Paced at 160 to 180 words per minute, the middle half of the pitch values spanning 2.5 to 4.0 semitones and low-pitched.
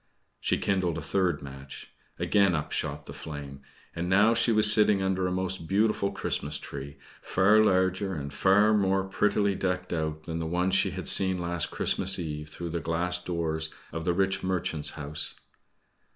Yes: average, 175 wpm; average, 3.3 semitones; very low, 90 Hz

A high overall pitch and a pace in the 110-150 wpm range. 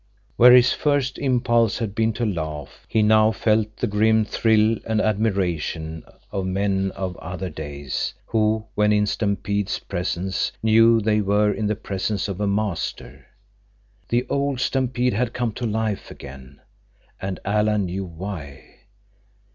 No: low, 105 Hz; average, 145 wpm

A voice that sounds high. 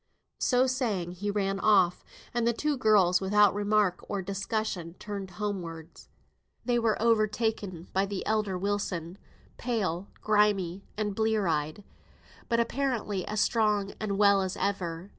Yes: high, 205 Hz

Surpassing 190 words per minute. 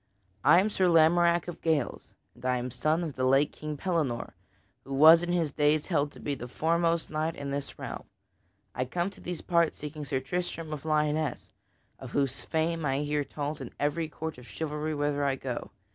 Yes: average, 200 wpm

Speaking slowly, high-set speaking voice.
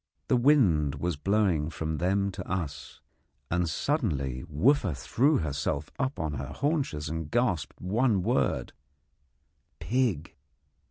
No: slow, 120 wpm; very low, 90 Hz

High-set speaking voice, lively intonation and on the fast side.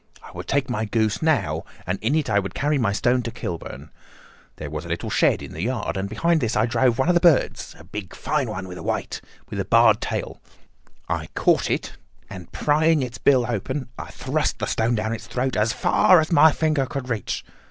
No: low, 115 Hz; wide, 5.7 semitones; fast, 215 wpm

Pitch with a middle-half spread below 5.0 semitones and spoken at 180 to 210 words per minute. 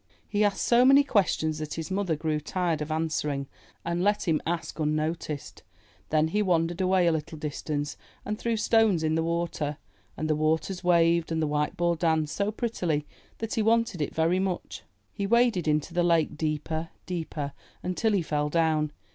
Yes: average, 3.4 semitones; average, 185 wpm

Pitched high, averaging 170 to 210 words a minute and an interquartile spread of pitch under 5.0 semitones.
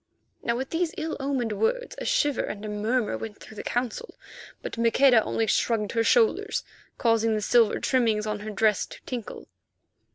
Yes: high, 230 Hz; average, 175 wpm; average, 3.8 semitones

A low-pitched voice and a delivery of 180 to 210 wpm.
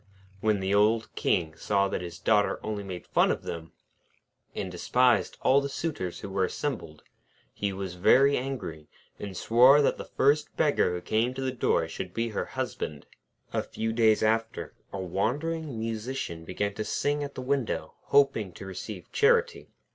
No: low, 110 Hz; average, 170 wpm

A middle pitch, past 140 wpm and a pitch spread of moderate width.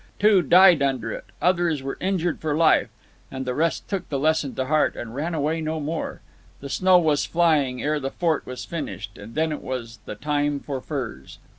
Yes: medium, 150 Hz; average, 200 wpm; average, 3.8 semitones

